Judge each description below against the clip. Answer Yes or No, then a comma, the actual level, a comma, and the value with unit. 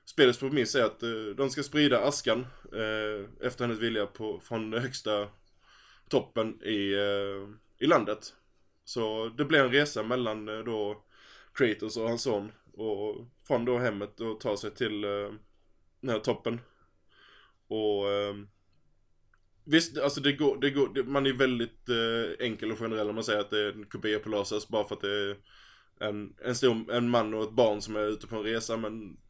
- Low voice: Yes, low, 110 Hz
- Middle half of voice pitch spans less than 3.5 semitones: Yes, average, 2.8 semitones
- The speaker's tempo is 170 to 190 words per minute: Yes, average, 185 wpm